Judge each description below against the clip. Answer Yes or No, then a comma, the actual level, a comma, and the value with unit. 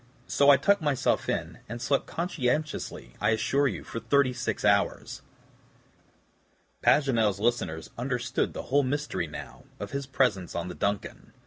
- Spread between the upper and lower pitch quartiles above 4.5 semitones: Yes, average, 5.3 semitones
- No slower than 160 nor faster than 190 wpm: No, average, 145 wpm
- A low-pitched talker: Yes, low, 125 Hz